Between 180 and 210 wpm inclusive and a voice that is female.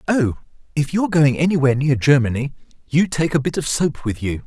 No: average, 200 wpm; male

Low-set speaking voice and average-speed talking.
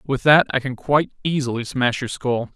No: low, 130 Hz; fast, 210 wpm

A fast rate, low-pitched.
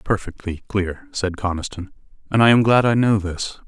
No: average, 180 wpm; low, 105 Hz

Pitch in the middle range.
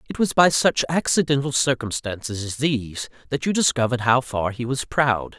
No: low, 130 Hz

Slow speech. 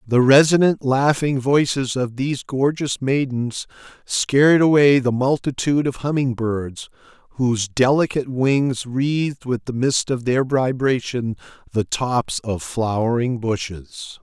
Yes: slow, 125 wpm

